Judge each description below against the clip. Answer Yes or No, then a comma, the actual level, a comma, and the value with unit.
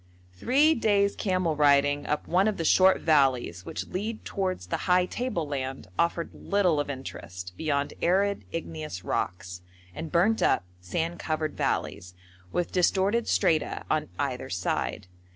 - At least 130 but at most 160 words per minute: Yes, average, 145 wpm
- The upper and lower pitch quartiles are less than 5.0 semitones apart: No, average, 5.3 semitones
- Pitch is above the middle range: No, medium, 160 Hz